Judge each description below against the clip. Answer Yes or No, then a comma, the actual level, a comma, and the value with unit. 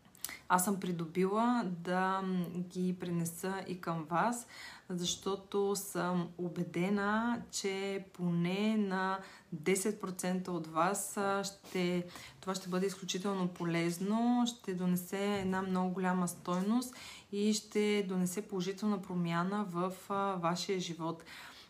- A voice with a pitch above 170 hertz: Yes, medium, 185 Hz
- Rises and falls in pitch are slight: Yes, narrow, 2.0 semitones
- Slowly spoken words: Yes, slow, 110 wpm